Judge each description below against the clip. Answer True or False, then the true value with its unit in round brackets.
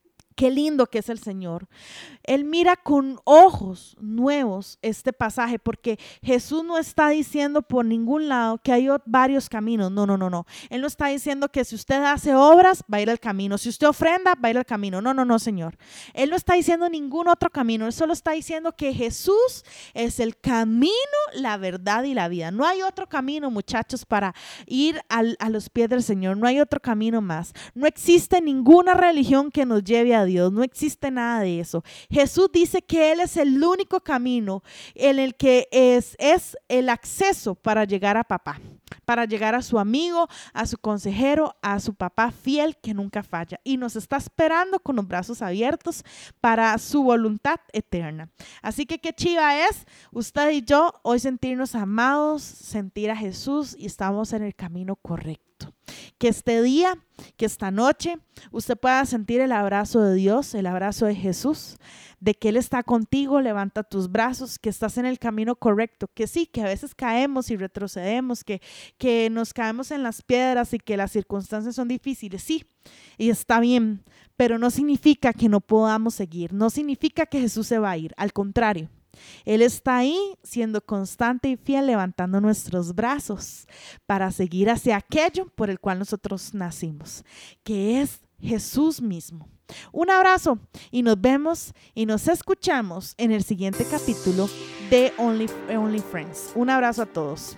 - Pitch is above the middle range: True (235 Hz)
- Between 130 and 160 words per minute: False (180 wpm)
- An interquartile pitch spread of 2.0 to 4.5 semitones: False (5.3 semitones)